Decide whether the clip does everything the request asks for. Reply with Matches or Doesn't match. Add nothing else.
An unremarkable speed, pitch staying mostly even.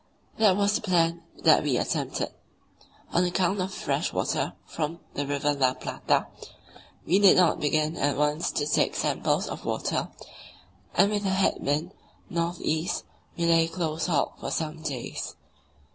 Doesn't match